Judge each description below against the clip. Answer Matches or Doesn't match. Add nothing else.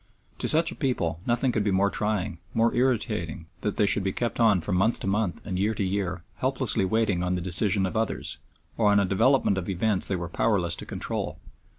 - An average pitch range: Matches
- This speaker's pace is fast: Matches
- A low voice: Matches